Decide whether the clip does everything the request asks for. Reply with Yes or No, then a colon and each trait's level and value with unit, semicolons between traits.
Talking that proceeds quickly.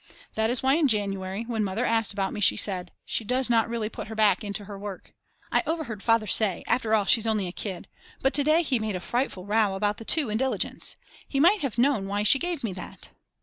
Yes: fast, 240 wpm